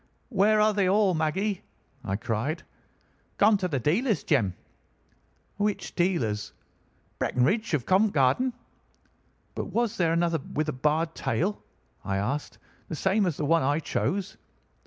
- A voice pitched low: No, medium, 170 Hz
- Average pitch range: No, wide, 6.0 semitones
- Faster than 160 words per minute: No, average, 140 wpm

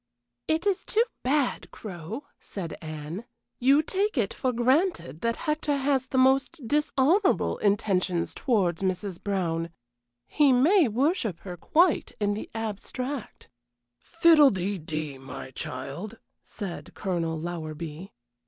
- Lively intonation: Yes, wide, 8.6 semitones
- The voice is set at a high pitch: Yes, high, 215 Hz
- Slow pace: Yes, slow, 125 wpm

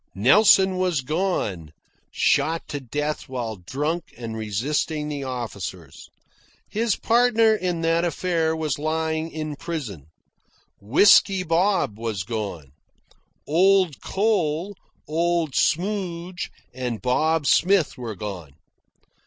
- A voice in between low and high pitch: Yes, medium, 155 Hz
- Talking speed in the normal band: No, slow, 105 wpm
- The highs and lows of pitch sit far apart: Yes, wide, 6.9 semitones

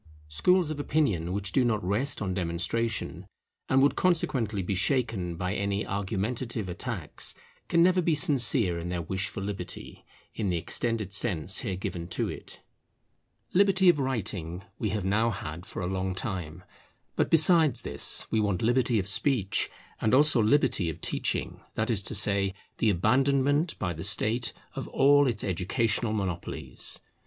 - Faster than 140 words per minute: Yes, average, 160 wpm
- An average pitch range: No, wide, 5.8 semitones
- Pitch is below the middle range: Yes, low, 105 Hz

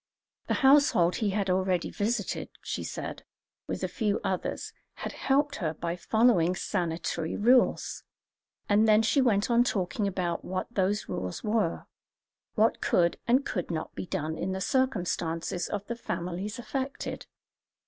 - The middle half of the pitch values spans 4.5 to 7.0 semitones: Yes, average, 4.8 semitones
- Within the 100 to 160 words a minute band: Yes, average, 150 wpm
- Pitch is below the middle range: No, high, 200 Hz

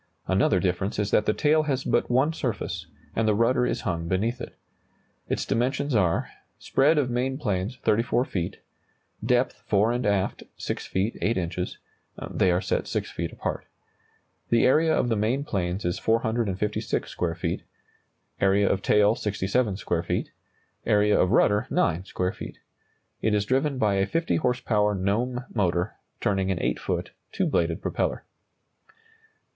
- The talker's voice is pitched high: No, low, 105 Hz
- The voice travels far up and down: No, average, 4.6 semitones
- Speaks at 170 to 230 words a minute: No, average, 160 wpm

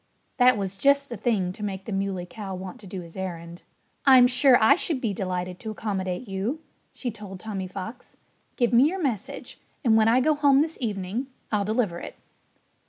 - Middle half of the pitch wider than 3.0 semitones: Yes, average, 4.8 semitones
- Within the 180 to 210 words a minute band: Yes, average, 195 wpm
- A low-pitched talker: No, high, 210 Hz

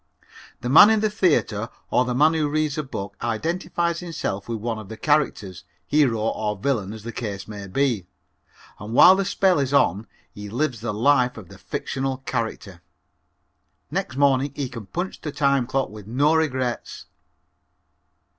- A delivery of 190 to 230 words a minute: No, average, 170 wpm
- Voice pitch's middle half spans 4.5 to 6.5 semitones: Yes, wide, 5.6 semitones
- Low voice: Yes, low, 130 Hz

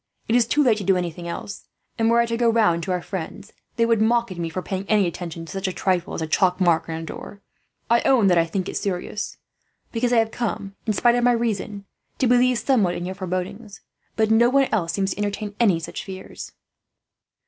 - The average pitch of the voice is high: Yes, high, 200 Hz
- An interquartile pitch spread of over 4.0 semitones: Yes, average, 4.4 semitones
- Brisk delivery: Yes, fast, 235 wpm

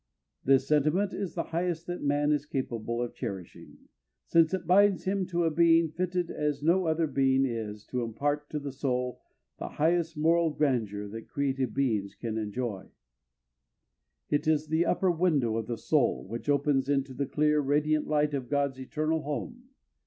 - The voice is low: No, medium, 145 Hz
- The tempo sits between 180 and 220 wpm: No, average, 170 wpm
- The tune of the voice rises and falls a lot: No, average, 4.1 semitones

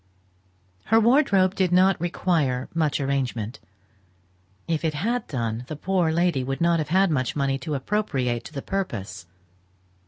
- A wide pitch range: Yes, wide, 6.0 semitones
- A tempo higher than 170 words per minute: No, average, 150 wpm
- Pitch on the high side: No, medium, 155 Hz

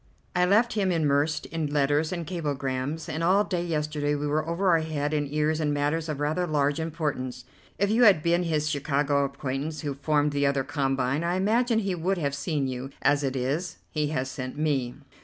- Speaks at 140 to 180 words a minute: No, average, 195 wpm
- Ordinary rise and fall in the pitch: Yes, average, 3.0 semitones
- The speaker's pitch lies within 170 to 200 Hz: No, medium, 150 Hz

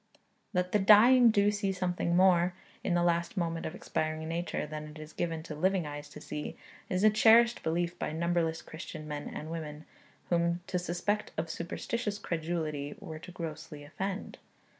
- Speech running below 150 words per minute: No, average, 175 wpm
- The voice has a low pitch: No, medium, 170 Hz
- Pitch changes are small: No, average, 3.2 semitones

